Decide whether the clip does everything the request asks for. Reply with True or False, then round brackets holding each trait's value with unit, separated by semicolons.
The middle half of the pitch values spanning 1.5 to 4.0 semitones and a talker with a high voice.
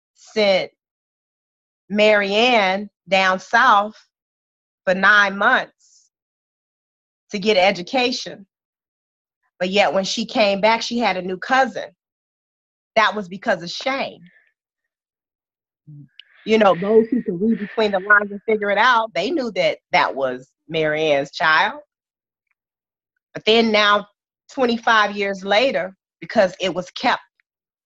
True (3.5 semitones; 205 Hz)